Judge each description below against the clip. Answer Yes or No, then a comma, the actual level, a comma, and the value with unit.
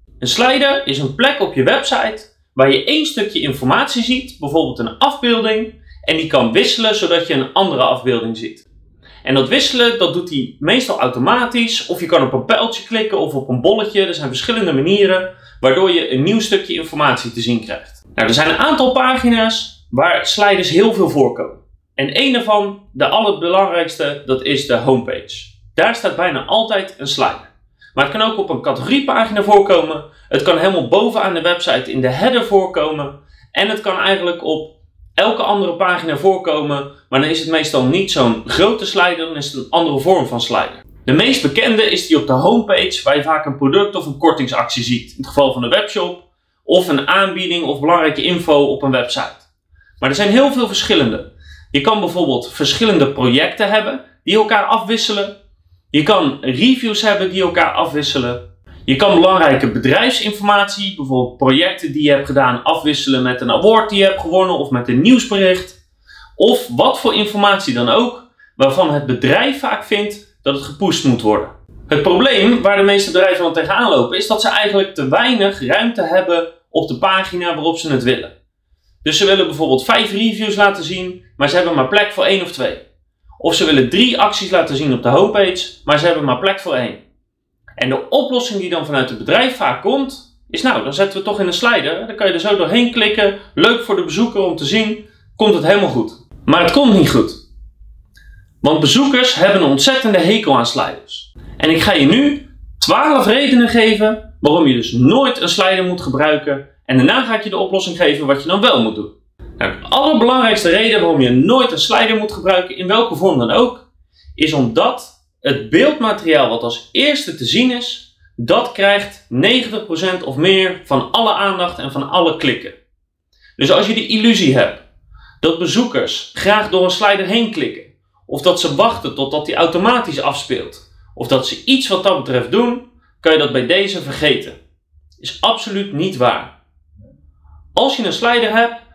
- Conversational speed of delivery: Yes, average, 190 wpm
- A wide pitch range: Yes, wide, 7.8 semitones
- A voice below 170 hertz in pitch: No, medium, 185 Hz